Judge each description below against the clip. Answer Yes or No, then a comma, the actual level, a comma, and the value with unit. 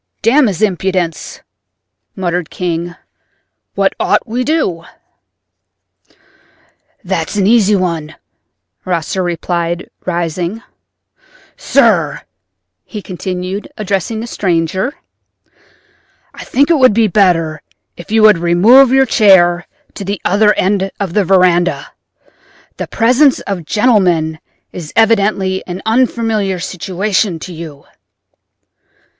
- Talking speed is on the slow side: Yes, slow, 105 wpm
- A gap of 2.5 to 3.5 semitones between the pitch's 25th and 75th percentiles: No, average, 3.9 semitones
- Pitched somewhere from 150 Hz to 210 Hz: Yes, high, 190 Hz